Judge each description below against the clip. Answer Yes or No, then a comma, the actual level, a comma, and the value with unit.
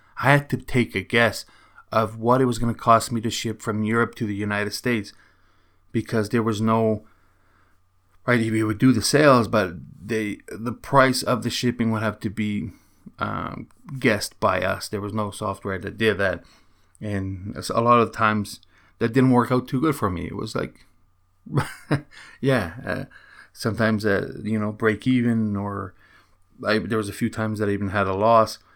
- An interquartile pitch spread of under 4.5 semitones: Yes, average, 2.8 semitones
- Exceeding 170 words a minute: Yes, average, 190 wpm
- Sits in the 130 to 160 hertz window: No, low, 110 Hz